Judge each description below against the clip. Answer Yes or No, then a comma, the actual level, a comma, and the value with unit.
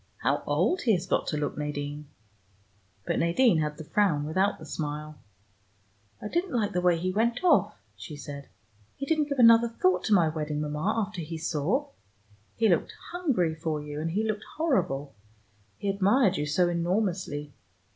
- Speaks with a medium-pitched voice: Yes, medium, 175 Hz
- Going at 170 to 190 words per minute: Yes, average, 175 wpm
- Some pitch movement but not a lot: No, wide, 6.5 semitones